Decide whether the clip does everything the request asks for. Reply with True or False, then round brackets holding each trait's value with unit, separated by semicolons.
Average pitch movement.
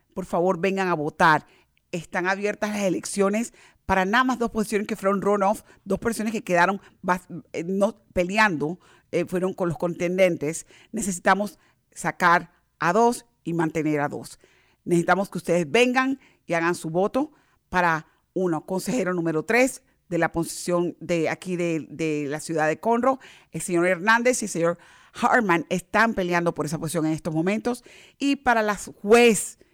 True (4.1 semitones)